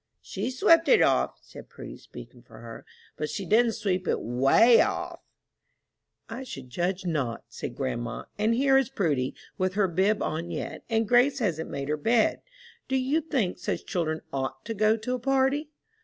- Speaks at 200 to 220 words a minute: No, average, 180 wpm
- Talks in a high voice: Yes, high, 210 Hz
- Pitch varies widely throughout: Yes, wide, 8.0 semitones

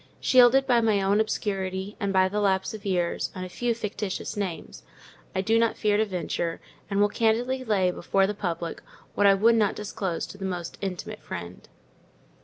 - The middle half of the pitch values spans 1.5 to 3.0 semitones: Yes, average, 2.7 semitones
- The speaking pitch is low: No, high, 200 Hz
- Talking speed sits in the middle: Yes, average, 190 wpm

